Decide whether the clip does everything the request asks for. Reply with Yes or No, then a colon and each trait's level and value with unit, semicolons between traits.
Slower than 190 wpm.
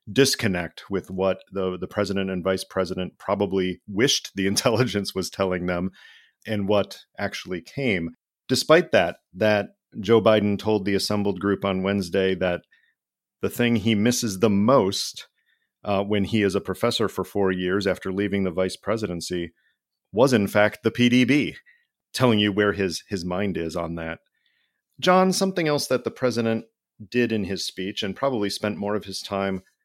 Yes: average, 165 wpm